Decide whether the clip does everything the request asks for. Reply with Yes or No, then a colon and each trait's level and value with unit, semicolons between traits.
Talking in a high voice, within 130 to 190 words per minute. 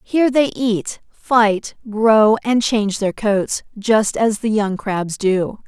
Yes: high, 215 Hz; average, 160 wpm